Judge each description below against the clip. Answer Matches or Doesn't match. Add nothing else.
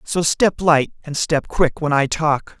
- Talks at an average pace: Doesn't match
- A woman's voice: Doesn't match